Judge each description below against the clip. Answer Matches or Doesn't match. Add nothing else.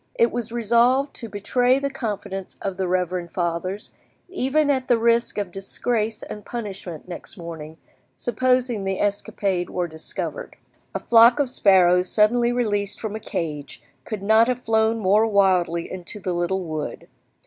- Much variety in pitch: Doesn't match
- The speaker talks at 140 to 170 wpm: Matches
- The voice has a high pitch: Matches